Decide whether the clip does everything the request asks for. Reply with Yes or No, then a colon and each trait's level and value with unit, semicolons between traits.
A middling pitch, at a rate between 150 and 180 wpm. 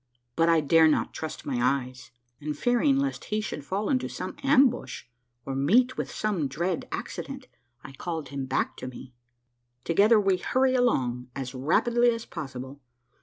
Yes: medium, 165 Hz; average, 165 wpm